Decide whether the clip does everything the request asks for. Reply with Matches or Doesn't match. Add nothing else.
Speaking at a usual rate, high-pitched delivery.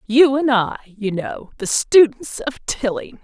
Matches